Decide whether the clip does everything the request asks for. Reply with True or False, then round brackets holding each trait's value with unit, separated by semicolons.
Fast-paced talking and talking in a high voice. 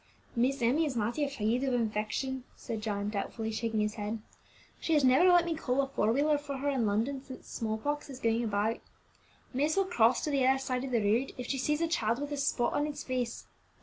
True (235 wpm; 255 Hz)